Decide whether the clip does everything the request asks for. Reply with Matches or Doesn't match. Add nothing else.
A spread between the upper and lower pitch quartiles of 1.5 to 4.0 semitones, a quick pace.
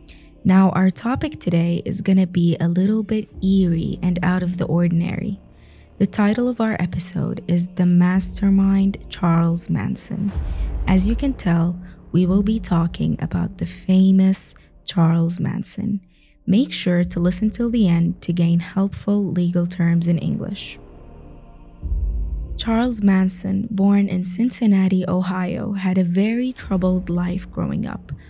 Matches